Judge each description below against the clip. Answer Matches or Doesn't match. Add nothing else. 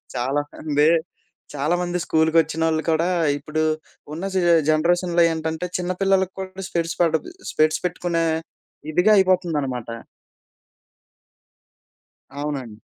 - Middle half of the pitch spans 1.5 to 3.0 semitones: Matches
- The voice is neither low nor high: Matches